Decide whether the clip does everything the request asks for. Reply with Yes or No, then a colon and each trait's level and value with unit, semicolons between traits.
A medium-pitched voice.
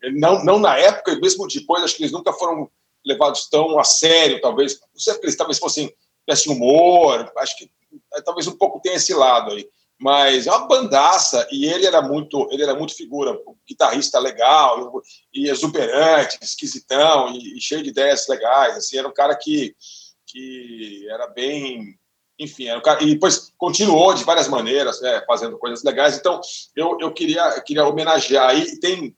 Yes: medium, 165 Hz